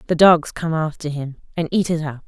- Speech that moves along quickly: Yes, fast, 240 wpm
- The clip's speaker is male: No, female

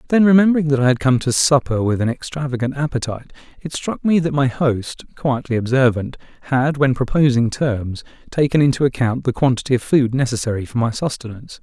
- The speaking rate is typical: Yes, average, 180 wpm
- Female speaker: No, male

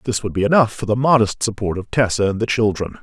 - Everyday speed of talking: No, fast, 260 wpm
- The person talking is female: No, male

